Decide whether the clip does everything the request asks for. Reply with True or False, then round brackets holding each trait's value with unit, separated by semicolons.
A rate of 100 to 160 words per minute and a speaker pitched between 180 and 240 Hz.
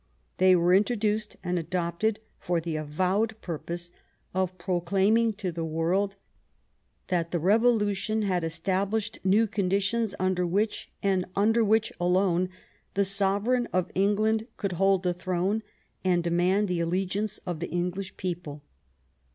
True (140 wpm; 190 Hz)